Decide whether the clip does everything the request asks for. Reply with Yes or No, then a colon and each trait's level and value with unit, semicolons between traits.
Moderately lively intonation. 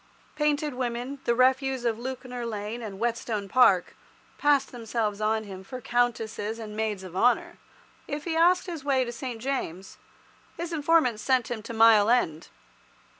Yes: average, 3.5 semitones